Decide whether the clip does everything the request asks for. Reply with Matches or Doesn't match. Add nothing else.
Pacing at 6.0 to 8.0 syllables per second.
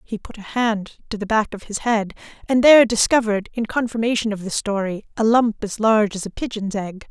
Doesn't match